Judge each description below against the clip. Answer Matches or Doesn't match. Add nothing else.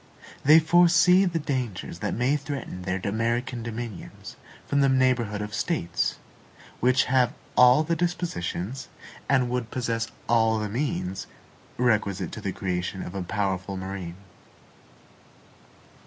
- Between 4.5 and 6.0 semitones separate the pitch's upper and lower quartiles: Matches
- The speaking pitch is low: Matches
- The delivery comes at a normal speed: Doesn't match